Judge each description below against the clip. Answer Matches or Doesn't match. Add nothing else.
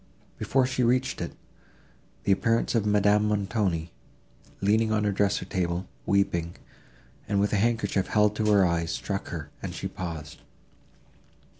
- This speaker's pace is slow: Doesn't match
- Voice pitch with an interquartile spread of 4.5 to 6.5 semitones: Doesn't match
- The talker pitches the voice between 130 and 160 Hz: Doesn't match